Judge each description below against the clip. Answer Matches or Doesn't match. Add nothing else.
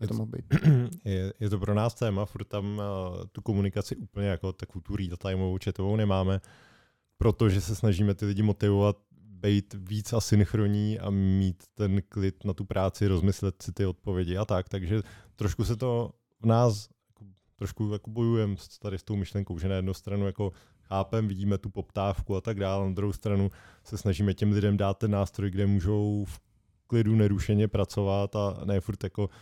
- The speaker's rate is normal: Doesn't match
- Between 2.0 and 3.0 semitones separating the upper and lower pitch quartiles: Doesn't match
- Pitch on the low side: Matches